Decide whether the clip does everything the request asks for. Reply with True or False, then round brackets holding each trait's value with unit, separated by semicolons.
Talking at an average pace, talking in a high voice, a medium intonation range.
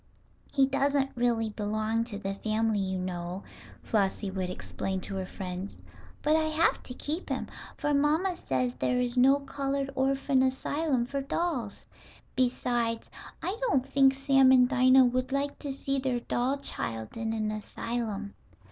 True (155 wpm; 250 Hz; 4.5 semitones)